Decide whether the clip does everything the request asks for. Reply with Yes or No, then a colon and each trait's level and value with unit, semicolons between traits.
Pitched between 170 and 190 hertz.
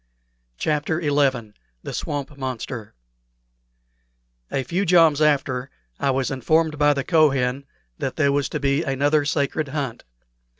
No: medium, 140 Hz